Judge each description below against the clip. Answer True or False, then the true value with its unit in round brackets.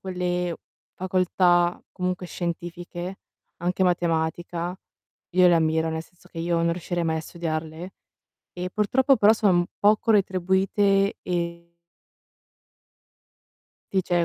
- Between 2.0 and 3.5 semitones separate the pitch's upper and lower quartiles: False (1.6 semitones)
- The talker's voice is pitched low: False (175 Hz)